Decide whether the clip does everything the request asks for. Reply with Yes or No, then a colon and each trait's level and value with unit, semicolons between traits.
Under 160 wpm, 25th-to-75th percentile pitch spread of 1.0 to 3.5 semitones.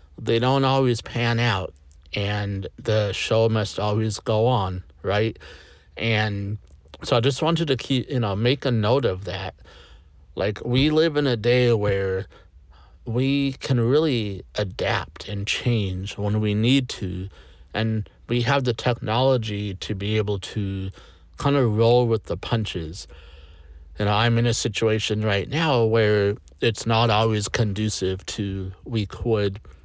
No: average, 150 wpm; average, 3.9 semitones